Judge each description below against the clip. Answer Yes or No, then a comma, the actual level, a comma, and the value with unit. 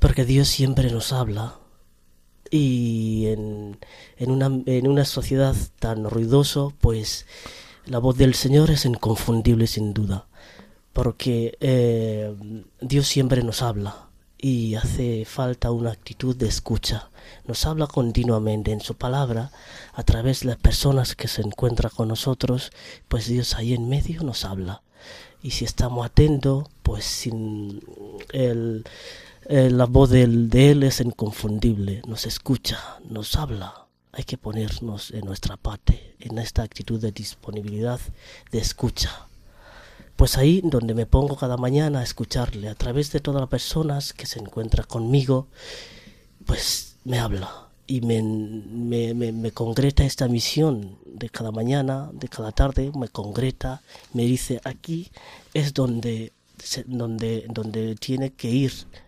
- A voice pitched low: Yes, low, 120 Hz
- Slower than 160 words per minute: Yes, average, 140 wpm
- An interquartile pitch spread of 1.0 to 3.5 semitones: Yes, average, 3.2 semitones